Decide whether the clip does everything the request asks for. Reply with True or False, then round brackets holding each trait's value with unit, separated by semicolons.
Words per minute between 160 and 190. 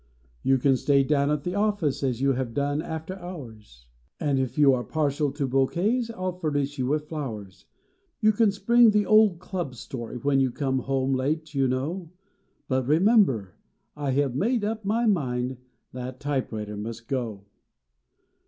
True (170 wpm)